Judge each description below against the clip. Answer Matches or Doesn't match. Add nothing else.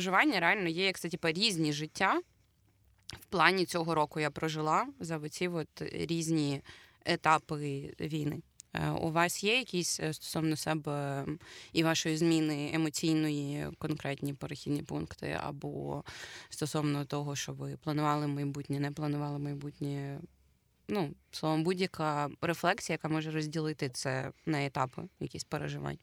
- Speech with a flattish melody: Matches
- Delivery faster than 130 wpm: Doesn't match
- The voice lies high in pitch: Doesn't match